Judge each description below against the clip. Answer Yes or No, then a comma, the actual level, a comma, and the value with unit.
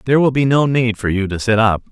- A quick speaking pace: Yes, fast, 315 wpm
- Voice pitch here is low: Yes, low, 115 Hz